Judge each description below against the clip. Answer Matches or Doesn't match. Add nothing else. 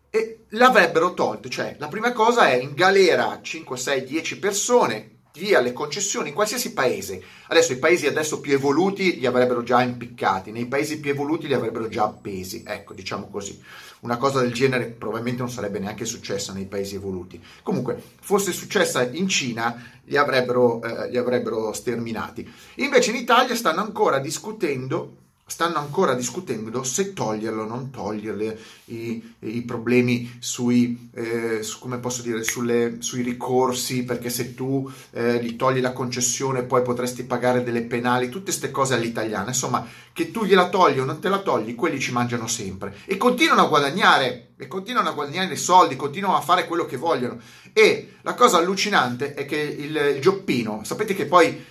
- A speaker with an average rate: Doesn't match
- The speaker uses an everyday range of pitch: Doesn't match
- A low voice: Matches